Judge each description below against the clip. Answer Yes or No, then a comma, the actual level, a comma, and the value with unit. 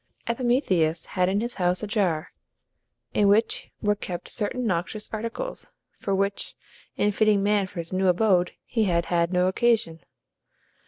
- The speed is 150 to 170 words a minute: Yes, average, 155 wpm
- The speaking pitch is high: Yes, high, 200 Hz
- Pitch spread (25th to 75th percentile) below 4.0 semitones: Yes, average, 3.3 semitones